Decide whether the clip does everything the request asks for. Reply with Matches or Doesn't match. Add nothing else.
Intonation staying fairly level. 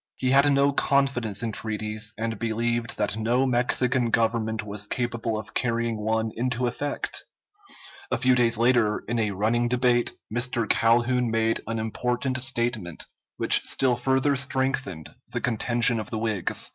Matches